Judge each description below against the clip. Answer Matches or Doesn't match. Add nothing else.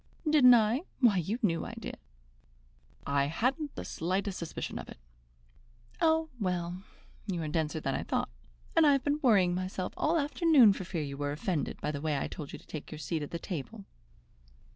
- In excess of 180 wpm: Matches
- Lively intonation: Matches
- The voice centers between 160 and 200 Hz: Matches